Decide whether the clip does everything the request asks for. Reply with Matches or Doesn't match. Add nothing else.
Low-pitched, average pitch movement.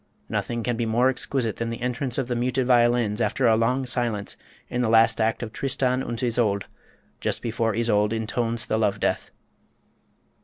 Doesn't match